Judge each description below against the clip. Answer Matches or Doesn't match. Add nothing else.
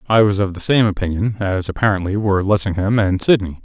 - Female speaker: Doesn't match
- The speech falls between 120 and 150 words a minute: Doesn't match